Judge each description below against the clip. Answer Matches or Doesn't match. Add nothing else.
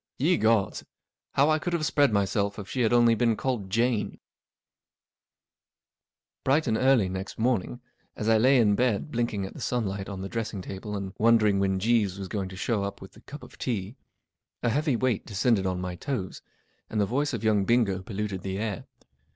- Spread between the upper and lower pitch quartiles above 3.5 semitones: Matches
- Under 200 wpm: Doesn't match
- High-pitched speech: Doesn't match